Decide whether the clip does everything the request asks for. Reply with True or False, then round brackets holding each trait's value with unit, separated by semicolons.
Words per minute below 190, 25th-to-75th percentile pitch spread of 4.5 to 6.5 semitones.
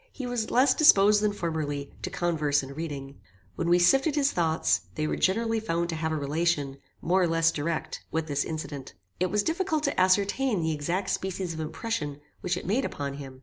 False (200 wpm; 5.4 semitones)